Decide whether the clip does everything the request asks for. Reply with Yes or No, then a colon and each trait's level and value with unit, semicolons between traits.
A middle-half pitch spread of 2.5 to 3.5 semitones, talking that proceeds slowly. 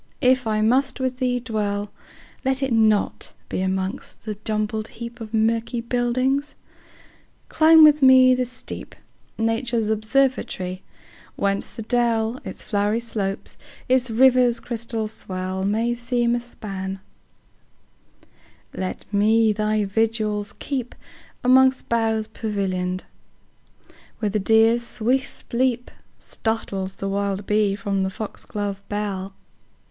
Yes: average, 3.2 semitones; slow, 105 wpm